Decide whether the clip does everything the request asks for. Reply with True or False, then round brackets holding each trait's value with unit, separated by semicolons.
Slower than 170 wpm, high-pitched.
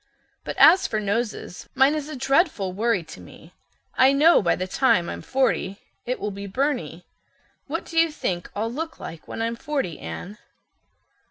False (175 wpm; 230 Hz)